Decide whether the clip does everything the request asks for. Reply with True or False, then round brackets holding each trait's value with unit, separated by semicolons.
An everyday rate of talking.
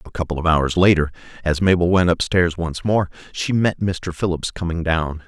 True (195 wpm)